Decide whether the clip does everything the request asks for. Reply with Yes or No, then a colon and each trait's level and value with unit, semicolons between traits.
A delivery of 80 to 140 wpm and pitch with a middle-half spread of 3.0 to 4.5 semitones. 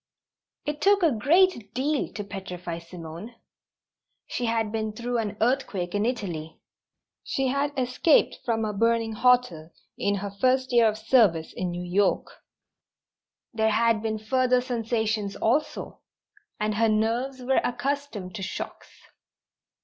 Yes: slow, 135 wpm; average, 3.8 semitones